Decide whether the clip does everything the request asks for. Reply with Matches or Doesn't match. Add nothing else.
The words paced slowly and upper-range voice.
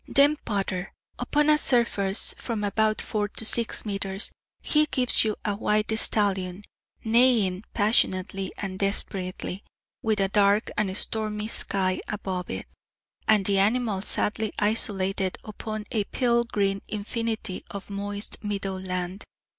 Matches